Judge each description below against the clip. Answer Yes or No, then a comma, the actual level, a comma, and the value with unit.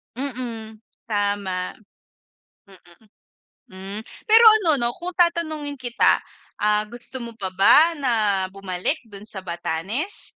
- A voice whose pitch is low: No, high, 230 Hz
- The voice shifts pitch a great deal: Yes, wide, 6.6 semitones